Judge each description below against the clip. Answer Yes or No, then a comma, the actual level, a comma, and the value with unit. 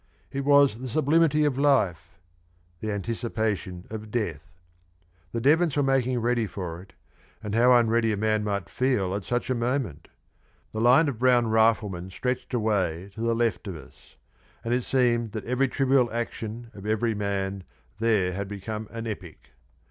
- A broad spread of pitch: No, average, 3.8 semitones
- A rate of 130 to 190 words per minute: Yes, average, 165 wpm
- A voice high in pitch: No, low, 115 Hz